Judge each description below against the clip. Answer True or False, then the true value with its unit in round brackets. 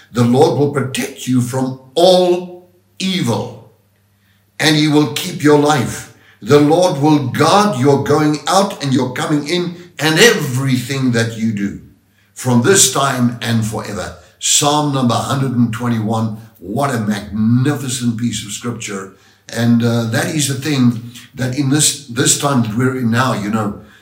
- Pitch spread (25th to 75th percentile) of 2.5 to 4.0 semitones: False (4.6 semitones)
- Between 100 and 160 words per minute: True (150 wpm)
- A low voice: True (130 Hz)